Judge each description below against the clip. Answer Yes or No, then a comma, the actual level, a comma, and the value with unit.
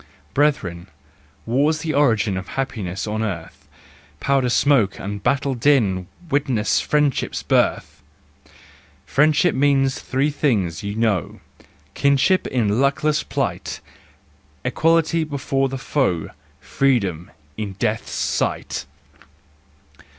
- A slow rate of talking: Yes, slow, 100 wpm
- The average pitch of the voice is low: Yes, low, 130 Hz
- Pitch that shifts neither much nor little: No, wide, 5.9 semitones